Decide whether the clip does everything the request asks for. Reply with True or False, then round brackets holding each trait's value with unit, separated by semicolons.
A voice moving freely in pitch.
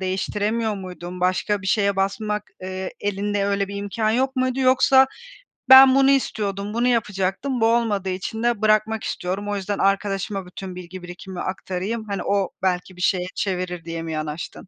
False (2.9 semitones)